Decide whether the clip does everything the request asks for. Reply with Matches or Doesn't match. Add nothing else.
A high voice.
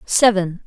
Matches